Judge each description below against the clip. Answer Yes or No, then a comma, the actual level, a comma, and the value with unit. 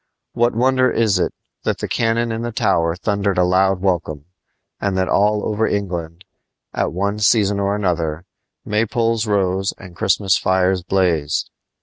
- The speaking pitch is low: Yes, low, 100 Hz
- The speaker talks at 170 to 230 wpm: No, average, 150 wpm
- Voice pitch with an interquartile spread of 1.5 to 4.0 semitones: Yes, average, 2.9 semitones